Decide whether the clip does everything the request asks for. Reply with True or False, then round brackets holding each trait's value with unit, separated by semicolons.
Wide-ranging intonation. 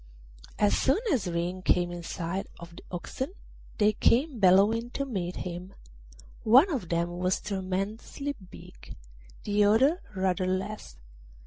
False (4.4 semitones)